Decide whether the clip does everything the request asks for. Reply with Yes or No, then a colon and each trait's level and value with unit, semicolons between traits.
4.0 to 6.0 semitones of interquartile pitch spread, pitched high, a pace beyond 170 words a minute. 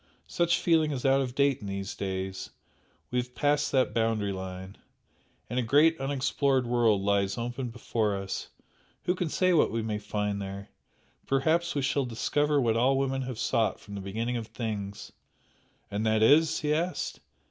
No: wide, 5.4 semitones; low, 120 Hz; average, 180 wpm